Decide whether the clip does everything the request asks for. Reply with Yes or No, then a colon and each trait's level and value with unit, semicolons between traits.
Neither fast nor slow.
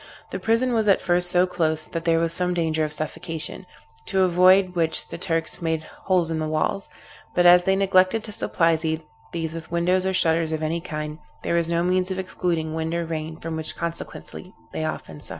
No: fast, 210 wpm